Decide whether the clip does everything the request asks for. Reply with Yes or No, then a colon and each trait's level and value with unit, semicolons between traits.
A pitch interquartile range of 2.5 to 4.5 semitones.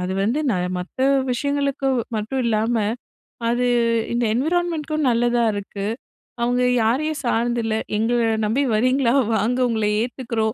Yes: average, 3.3 semitones